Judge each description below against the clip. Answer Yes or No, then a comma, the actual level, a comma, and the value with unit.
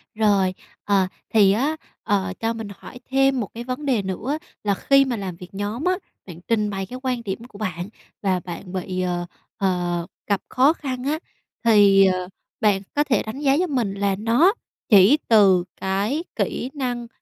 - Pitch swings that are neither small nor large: Yes, average, 4.9 semitones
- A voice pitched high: Yes, high, 210 Hz